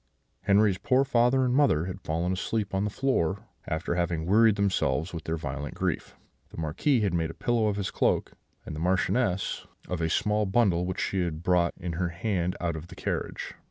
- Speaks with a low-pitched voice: Yes, very low, 90 Hz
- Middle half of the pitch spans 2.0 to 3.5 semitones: No, average, 4.0 semitones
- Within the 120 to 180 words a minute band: No, average, 200 wpm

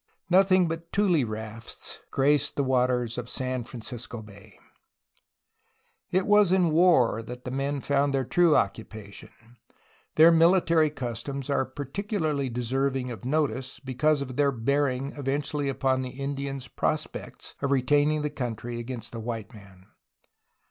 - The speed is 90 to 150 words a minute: Yes, average, 140 wpm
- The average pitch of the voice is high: No, low, 135 Hz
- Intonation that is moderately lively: Yes, average, 3.4 semitones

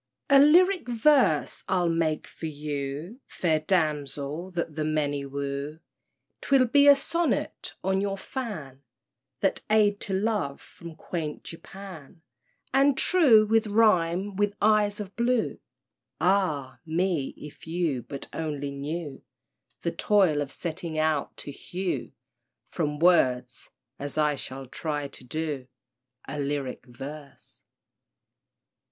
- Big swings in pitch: Yes, wide, 6.0 semitones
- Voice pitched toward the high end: No, medium, 165 Hz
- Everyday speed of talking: No, slow, 125 wpm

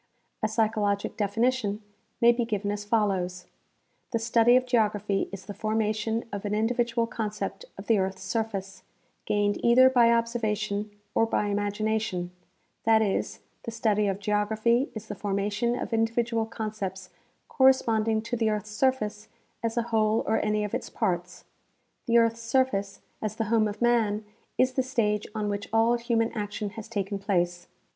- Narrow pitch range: Yes, narrow, 2.0 semitones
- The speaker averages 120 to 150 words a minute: No, average, 160 wpm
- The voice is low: No, high, 215 Hz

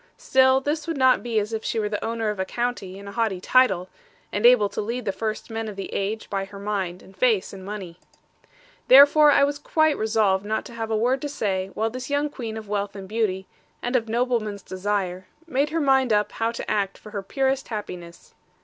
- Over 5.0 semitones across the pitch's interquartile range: No, average, 4.2 semitones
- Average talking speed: No, fast, 225 wpm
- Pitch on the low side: No, high, 220 Hz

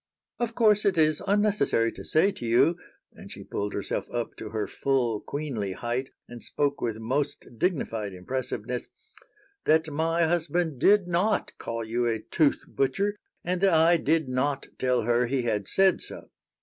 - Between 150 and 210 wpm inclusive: Yes, average, 165 wpm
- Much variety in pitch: Yes, wide, 6.5 semitones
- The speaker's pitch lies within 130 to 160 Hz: Yes, medium, 140 Hz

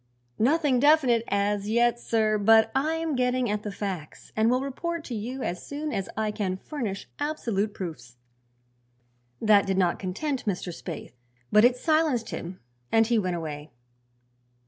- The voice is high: Yes, high, 220 Hz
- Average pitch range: Yes, average, 5.0 semitones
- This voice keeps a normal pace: Yes, average, 160 wpm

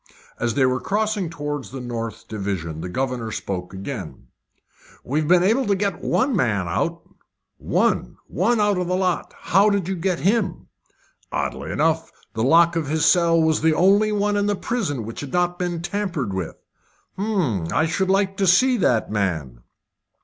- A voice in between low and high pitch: Yes, medium, 165 Hz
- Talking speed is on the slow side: No, average, 170 wpm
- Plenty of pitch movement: Yes, wide, 8.3 semitones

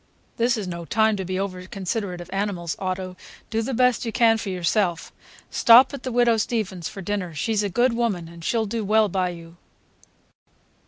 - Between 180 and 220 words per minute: Yes, average, 195 wpm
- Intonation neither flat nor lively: Yes, average, 3.8 semitones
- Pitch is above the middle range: Yes, high, 200 Hz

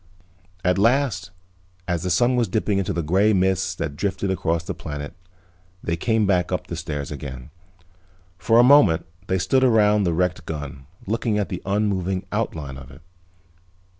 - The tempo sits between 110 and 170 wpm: Yes, average, 165 wpm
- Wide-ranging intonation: No, average, 4.5 semitones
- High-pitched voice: No, very low, 95 Hz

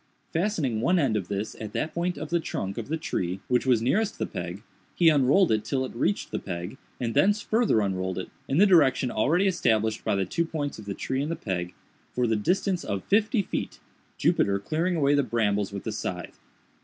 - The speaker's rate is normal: No, fast, 215 wpm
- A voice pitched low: Yes, low, 125 Hz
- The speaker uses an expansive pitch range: Yes, wide, 8.5 semitones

